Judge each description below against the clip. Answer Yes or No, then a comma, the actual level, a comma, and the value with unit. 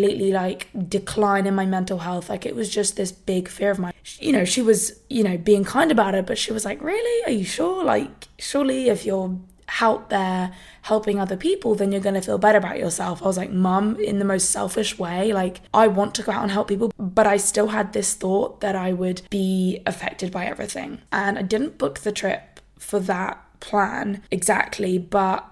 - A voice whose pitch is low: No, high, 200 Hz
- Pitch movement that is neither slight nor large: No, narrow, 2.3 semitones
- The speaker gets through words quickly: Yes, fast, 215 wpm